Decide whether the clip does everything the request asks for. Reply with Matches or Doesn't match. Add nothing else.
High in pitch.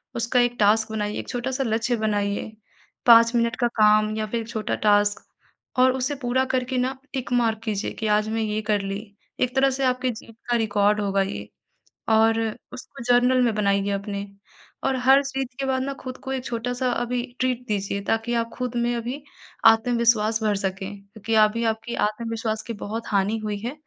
Matches